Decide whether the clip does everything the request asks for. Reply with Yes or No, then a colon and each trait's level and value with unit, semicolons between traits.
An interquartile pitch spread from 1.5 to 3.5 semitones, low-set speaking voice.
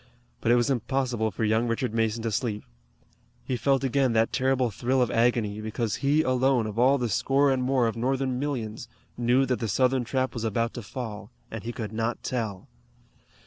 Yes: average, 2.7 semitones; low, 120 Hz